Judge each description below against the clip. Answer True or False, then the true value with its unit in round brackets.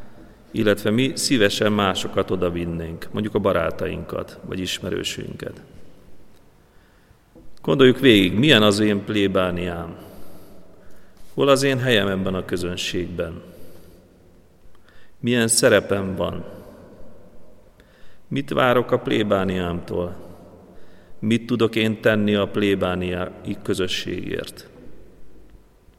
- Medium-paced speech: False (90 wpm)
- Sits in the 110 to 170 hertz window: False (95 Hz)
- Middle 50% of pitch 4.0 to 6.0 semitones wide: False (3.3 semitones)